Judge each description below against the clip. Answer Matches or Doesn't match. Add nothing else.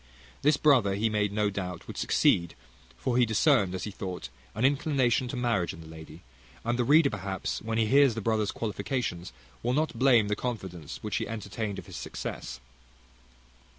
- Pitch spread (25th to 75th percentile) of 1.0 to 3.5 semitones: Doesn't match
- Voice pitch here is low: Matches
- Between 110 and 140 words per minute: Doesn't match